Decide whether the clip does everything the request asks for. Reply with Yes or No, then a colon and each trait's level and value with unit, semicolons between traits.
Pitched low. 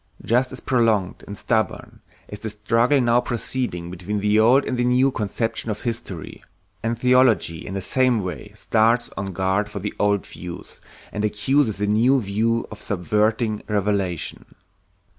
Yes: low, 110 Hz